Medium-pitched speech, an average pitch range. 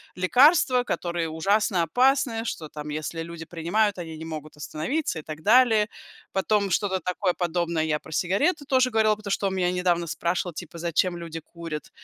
Yes: medium, 180 Hz; average, 4.7 semitones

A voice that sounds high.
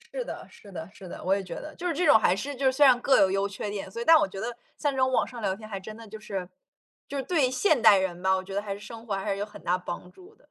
Yes: high, 210 Hz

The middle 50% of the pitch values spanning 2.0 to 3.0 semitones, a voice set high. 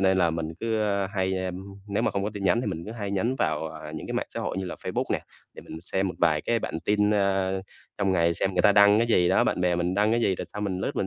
No: narrow, 2.6 semitones; very low, 95 Hz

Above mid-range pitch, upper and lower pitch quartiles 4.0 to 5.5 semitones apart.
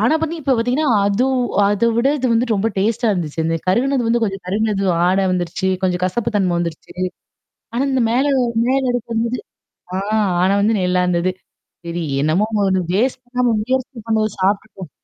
Yes: high, 215 Hz; average, 4.8 semitones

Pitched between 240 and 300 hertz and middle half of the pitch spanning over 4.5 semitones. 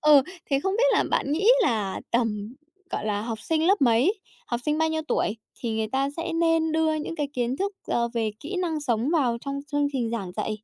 Yes: very high, 275 Hz; wide, 5.6 semitones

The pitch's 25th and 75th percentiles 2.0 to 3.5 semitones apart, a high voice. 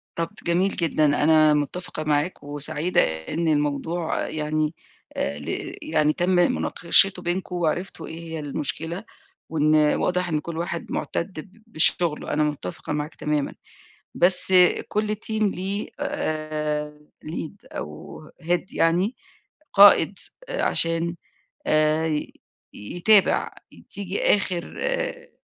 No: average, 3.0 semitones; medium, 165 Hz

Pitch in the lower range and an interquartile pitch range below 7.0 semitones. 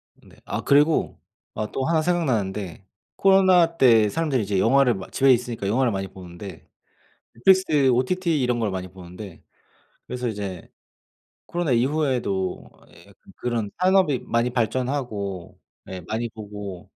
Yes: low, 120 Hz; wide, 6.3 semitones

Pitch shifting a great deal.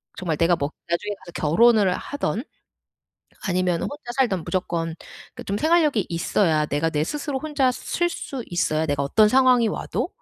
Yes: wide, 7.6 semitones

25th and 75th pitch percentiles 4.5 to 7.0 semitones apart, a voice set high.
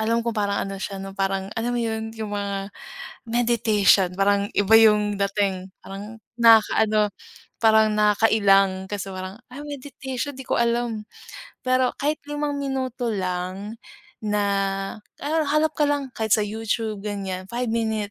No: average, 3.1 semitones; high, 215 Hz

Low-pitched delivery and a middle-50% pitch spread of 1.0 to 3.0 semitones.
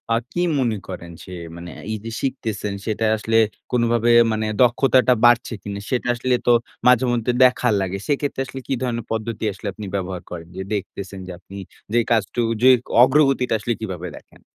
No: low, 115 Hz; average, 3.9 semitones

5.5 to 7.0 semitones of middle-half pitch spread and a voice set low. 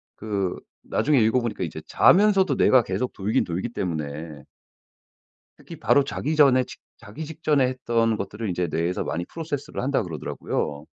No: wide, 7.7 semitones; low, 115 Hz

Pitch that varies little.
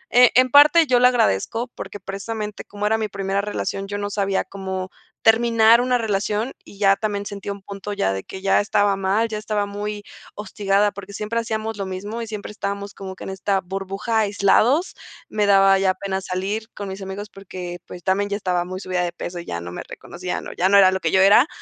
Yes: narrow, 2.0 semitones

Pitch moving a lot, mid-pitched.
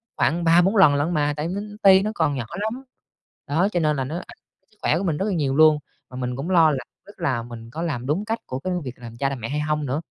No: average, 4.7 semitones; medium, 150 Hz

